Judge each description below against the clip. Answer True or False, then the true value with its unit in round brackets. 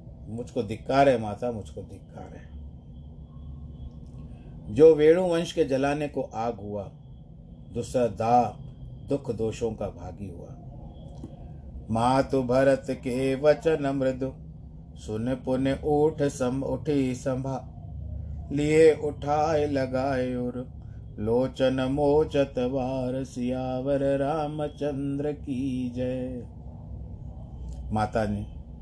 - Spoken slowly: True (95 wpm)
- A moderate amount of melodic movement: True (4.6 semitones)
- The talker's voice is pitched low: True (130 Hz)